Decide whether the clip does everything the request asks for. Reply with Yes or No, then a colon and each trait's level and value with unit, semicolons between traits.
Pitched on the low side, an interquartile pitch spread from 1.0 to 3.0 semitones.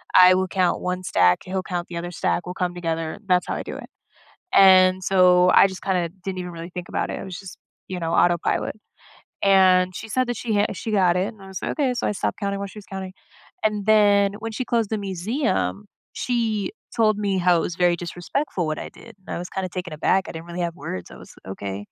No: medium, 185 Hz; narrow, 2.4 semitones